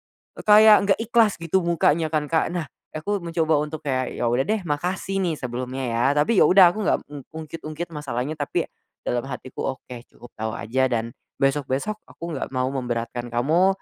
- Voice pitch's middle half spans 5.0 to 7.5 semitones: Yes, wide, 5.6 semitones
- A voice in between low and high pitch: Yes, medium, 150 Hz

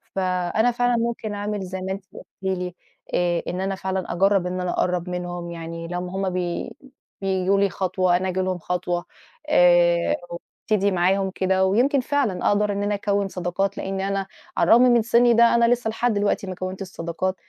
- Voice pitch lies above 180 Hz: Yes, high, 190 Hz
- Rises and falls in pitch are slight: Yes, narrow, 2.3 semitones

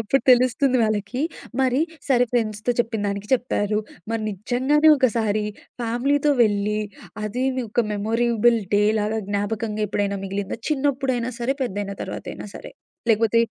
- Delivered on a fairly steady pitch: No, average, 3.3 semitones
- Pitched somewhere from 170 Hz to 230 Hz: Yes, high, 225 Hz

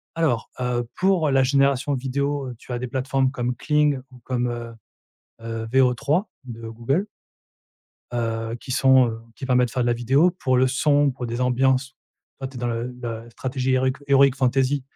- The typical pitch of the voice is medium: No, low, 130 Hz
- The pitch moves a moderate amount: No, narrow, 2.3 semitones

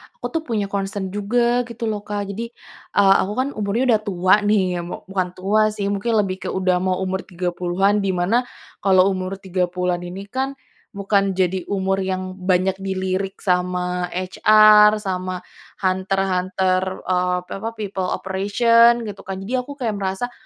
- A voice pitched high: Yes, high, 195 Hz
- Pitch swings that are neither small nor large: No, narrow, 2.1 semitones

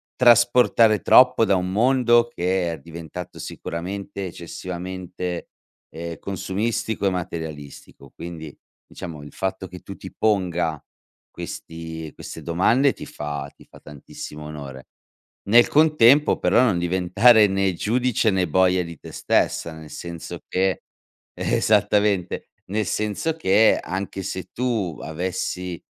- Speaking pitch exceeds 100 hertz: No, very low, 95 Hz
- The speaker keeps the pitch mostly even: No, average, 4.2 semitones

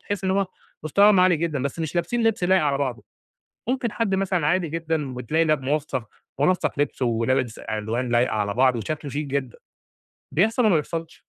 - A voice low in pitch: No, medium, 155 Hz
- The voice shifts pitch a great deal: Yes, wide, 6.0 semitones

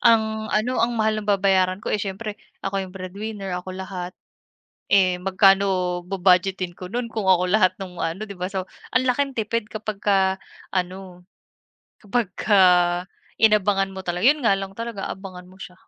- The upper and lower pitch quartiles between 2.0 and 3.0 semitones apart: Yes, narrow, 2.6 semitones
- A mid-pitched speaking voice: No, high, 195 Hz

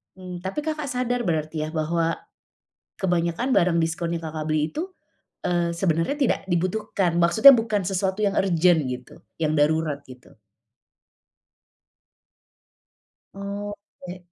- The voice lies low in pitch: No, medium, 175 Hz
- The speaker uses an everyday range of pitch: Yes, average, 4.0 semitones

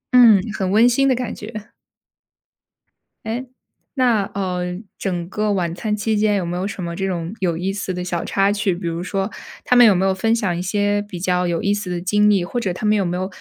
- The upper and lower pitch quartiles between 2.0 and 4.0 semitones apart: Yes, average, 2.8 semitones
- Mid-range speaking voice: No, high, 195 Hz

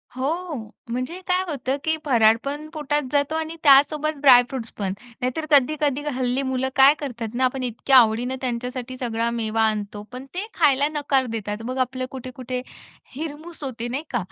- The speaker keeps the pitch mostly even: No, average, 3.2 semitones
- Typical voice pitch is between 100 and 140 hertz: No, very high, 260 Hz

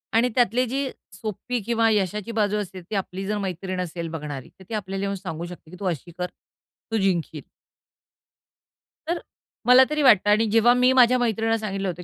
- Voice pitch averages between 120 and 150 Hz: No, high, 205 Hz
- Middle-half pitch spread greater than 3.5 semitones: Yes, average, 4.2 semitones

